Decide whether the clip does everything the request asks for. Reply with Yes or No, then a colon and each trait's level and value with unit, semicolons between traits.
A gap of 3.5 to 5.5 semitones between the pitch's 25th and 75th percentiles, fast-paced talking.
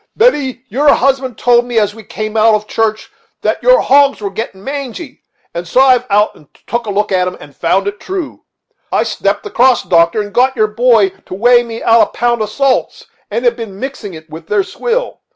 Yes: average, 4.2 semitones; fast, 225 wpm